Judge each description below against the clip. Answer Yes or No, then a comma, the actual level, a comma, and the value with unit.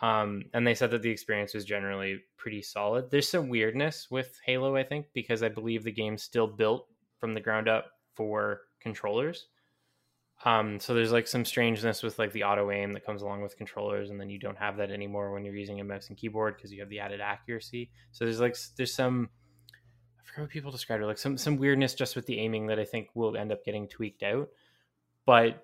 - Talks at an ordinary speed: No, fast, 225 wpm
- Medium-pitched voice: No, low, 110 Hz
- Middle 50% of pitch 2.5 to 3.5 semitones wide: Yes, average, 2.9 semitones